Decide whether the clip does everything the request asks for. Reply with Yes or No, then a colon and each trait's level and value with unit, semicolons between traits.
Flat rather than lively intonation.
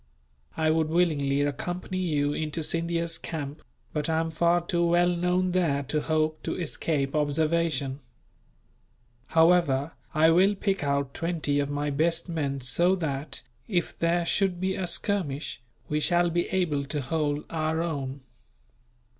No: average, 3.0 semitones